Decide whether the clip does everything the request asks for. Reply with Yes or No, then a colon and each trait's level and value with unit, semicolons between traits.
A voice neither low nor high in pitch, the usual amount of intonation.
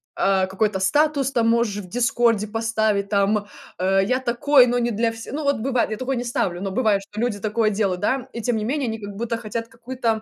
No: high, 225 Hz; average, 3.1 semitones